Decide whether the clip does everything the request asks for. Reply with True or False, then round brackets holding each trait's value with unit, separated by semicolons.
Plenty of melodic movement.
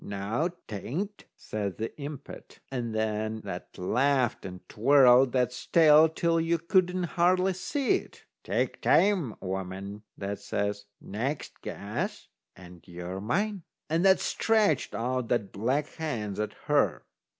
True (8.3 semitones)